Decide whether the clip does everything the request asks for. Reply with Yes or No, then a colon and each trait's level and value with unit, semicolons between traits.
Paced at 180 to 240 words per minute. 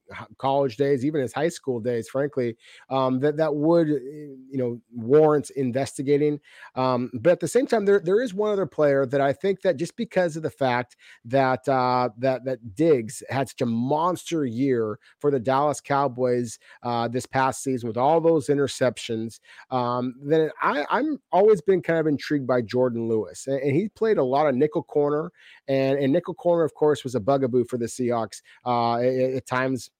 Yes: average, 190 wpm